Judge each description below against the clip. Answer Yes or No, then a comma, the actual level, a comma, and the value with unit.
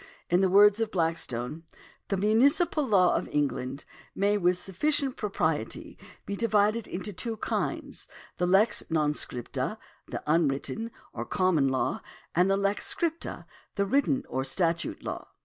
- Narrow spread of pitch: No, average, 4.9 semitones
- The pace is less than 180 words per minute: Yes, average, 155 wpm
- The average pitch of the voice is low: No, high, 195 Hz